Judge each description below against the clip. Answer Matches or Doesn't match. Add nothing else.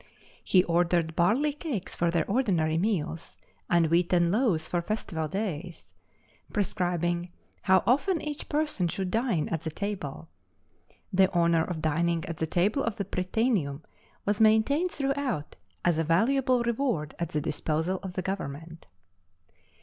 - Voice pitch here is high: Doesn't match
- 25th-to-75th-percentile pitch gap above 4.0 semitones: Matches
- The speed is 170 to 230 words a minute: Doesn't match